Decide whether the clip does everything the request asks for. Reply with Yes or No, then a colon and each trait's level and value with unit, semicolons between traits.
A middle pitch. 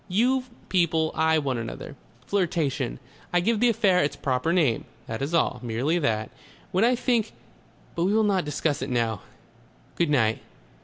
Yes: medium, 160 Hz